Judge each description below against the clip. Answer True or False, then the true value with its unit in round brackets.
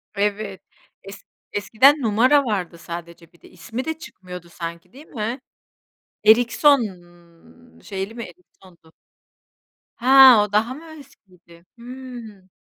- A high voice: True (215 Hz)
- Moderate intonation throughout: False (5.9 semitones)